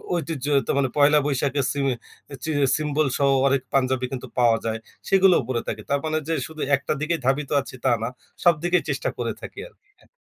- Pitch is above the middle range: No, medium, 140 Hz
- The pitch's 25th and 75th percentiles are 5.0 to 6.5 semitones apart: No, average, 3.3 semitones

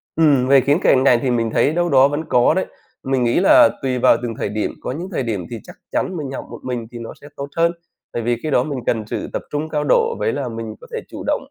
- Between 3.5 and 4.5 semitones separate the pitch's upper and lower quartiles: Yes, average, 3.8 semitones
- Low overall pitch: Yes, low, 130 Hz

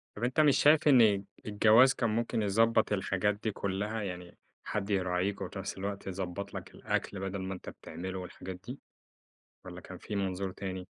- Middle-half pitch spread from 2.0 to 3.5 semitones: Yes, average, 2.8 semitones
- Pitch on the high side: No, low, 100 Hz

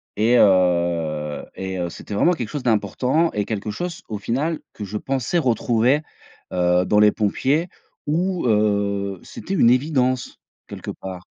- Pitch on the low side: Yes, low, 110 Hz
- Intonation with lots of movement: Yes, wide, 5.7 semitones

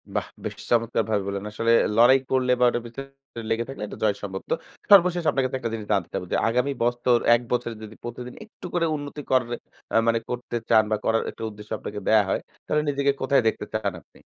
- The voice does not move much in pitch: No, average, 3.5 semitones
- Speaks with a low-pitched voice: Yes, low, 120 Hz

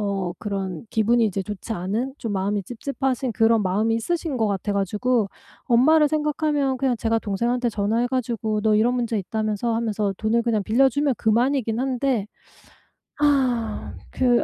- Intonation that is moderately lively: Yes, average, 3.4 semitones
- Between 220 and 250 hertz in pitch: Yes, high, 230 Hz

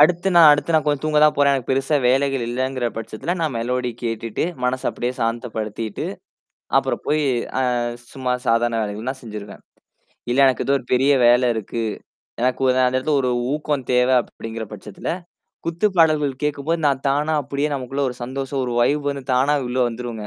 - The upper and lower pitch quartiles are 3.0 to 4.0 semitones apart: Yes, average, 3.3 semitones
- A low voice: Yes, low, 130 Hz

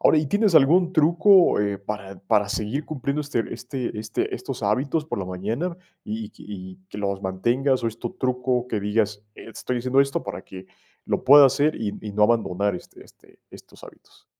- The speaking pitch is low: Yes, low, 115 Hz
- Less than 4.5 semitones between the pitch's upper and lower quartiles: No, wide, 5.6 semitones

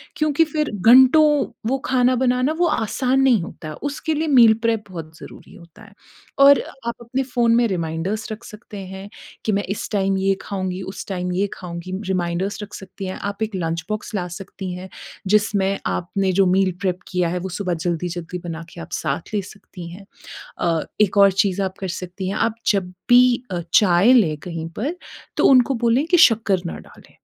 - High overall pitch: Yes, high, 200 Hz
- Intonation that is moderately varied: Yes, average, 4.5 semitones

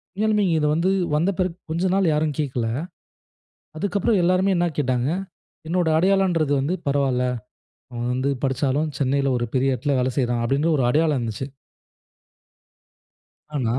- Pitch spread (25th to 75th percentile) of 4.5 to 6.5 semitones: Yes, average, 5.2 semitones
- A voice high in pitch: No, medium, 145 Hz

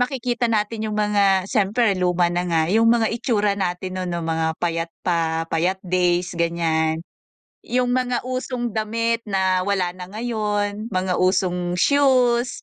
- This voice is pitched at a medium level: No, high, 195 Hz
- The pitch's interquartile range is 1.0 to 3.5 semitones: No, average, 4.4 semitones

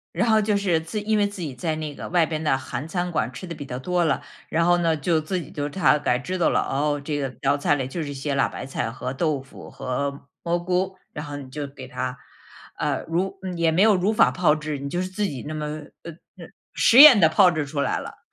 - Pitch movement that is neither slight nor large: Yes, average, 4.2 semitones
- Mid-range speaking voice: Yes, medium, 155 Hz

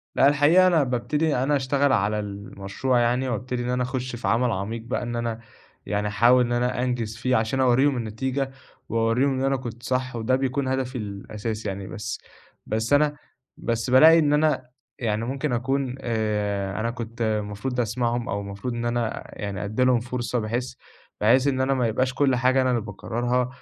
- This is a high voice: No, low, 120 Hz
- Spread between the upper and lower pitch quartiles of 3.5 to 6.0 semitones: No, average, 2.8 semitones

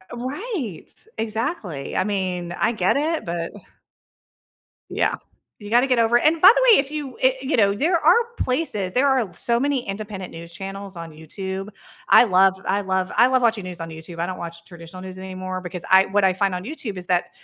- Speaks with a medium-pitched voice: No, high, 195 Hz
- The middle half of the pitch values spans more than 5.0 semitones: Yes, wide, 5.4 semitones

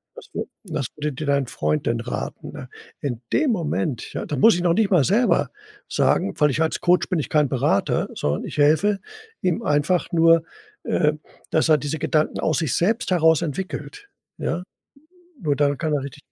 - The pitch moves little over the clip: No, average, 3.6 semitones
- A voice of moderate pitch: Yes, medium, 155 Hz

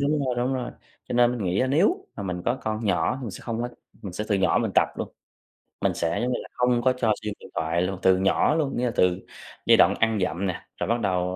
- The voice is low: Yes, low, 110 Hz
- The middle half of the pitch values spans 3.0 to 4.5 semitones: No, average, 5.1 semitones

